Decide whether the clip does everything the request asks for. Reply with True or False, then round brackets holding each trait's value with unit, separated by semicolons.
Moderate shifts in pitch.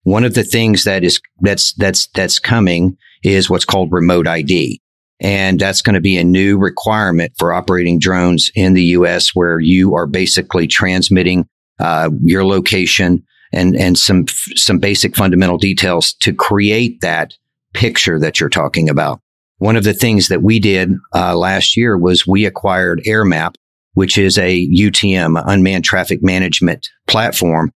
False (2.0 semitones)